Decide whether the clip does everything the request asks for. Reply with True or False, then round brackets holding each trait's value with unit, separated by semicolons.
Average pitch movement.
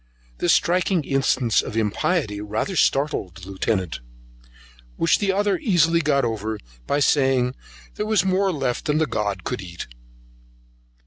False (8.3 semitones)